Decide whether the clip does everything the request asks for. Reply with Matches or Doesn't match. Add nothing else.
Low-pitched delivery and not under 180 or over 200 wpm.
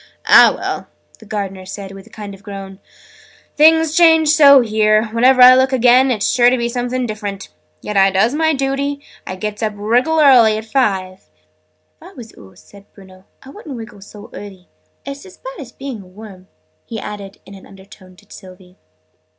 Doesn't match